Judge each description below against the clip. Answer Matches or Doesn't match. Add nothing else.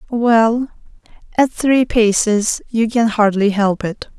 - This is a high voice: Matches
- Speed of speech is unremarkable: Doesn't match